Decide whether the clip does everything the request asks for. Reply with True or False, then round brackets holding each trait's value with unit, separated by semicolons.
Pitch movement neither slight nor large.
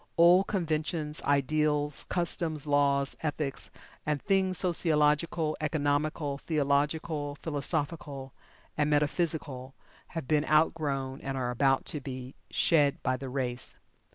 False (2.3 semitones)